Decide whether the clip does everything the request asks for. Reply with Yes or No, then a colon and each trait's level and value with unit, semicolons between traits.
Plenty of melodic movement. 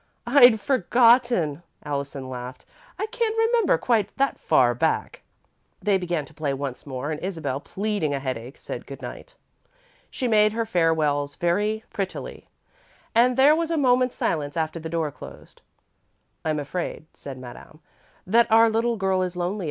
Yes: wide, 8.2 semitones